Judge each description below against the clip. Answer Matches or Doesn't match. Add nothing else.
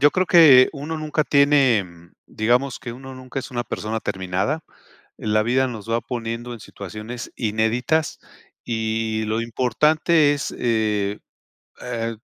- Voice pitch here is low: Matches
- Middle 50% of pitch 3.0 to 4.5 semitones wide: Matches